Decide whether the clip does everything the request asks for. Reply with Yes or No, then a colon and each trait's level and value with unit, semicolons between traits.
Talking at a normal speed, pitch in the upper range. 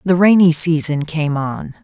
No: average, 165 wpm; medium, 160 Hz